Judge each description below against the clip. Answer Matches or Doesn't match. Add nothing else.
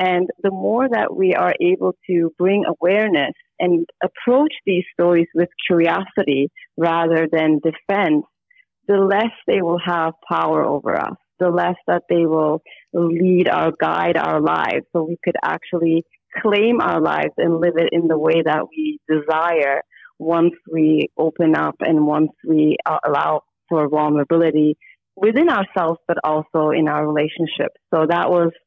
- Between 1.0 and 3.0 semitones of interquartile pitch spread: Matches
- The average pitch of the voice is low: Doesn't match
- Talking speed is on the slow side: Doesn't match